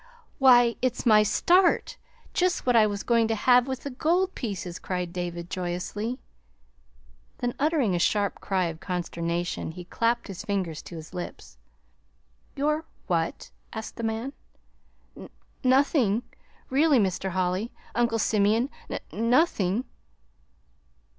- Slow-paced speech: Yes, slow, 130 wpm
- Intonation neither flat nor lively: No, wide, 5.7 semitones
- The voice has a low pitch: No, high, 220 Hz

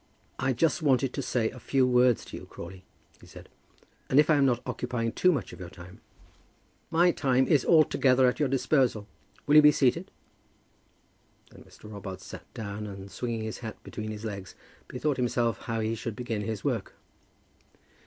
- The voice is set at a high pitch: No, low, 125 Hz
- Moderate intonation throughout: Yes, average, 4.0 semitones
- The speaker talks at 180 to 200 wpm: Yes, average, 185 wpm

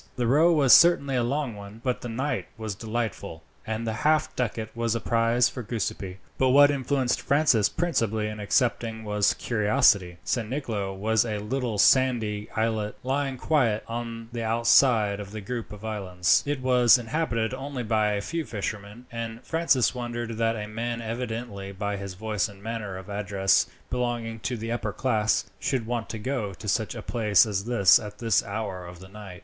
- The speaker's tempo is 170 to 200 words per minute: Yes, average, 185 wpm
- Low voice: Yes, low, 115 Hz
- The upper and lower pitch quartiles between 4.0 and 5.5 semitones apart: No, average, 2.9 semitones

